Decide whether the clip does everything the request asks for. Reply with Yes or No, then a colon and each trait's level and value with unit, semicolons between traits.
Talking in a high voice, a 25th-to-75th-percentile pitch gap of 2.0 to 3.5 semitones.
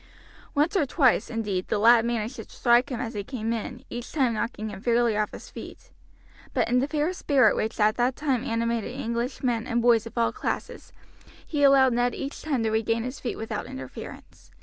Yes: high, 240 Hz; narrow, 2.5 semitones